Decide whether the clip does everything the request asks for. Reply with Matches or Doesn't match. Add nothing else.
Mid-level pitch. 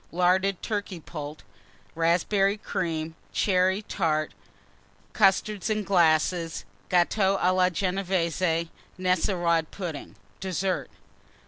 Matches